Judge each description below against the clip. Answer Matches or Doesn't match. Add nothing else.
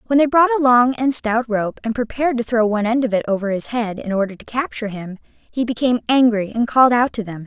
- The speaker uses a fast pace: Matches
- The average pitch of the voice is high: Matches